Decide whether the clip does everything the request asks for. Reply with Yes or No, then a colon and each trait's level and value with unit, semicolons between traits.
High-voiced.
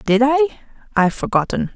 Yes: high, 245 Hz